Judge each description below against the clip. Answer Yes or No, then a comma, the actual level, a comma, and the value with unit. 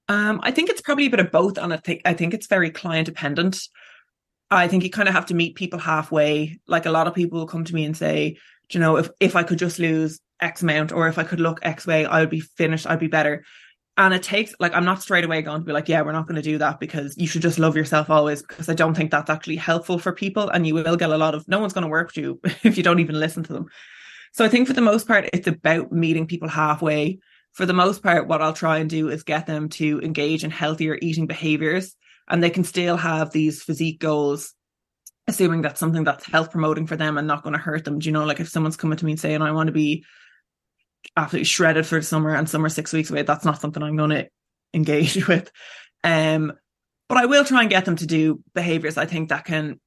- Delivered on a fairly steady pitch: Yes, narrow, 2.2 semitones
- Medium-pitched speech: Yes, medium, 160 Hz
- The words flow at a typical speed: No, fast, 265 wpm